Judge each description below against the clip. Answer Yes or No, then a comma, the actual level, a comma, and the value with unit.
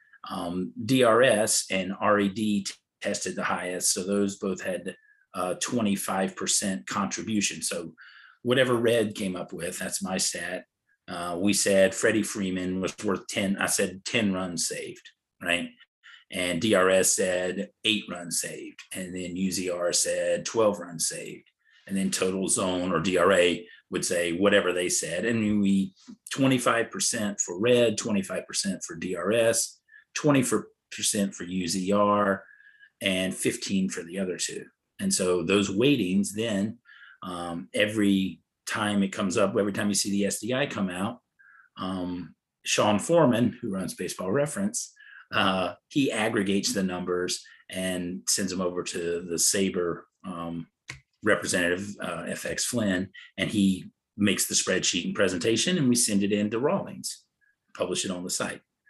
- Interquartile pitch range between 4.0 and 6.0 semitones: No, average, 3.5 semitones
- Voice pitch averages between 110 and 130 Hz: No, low, 100 Hz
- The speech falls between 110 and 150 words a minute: Yes, average, 145 wpm